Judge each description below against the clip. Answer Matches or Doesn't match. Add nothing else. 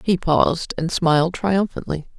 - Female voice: Matches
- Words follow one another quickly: Doesn't match